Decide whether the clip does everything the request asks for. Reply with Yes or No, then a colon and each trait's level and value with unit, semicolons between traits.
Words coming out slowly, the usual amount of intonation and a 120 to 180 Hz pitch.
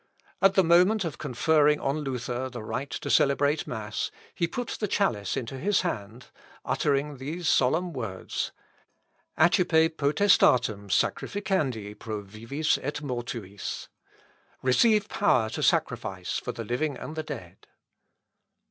No: slow, 130 wpm; wide, 6.0 semitones; medium, 140 Hz